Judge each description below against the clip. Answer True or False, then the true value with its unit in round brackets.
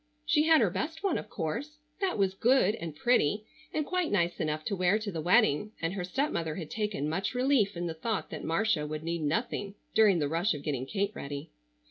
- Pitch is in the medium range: False (195 Hz)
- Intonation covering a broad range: True (6.4 semitones)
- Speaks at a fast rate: True (215 wpm)